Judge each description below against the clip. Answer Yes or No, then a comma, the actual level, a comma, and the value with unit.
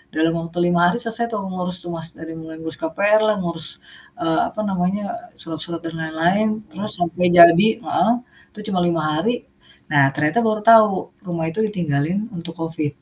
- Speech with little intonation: No, average, 3.8 semitones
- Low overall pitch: No, medium, 170 Hz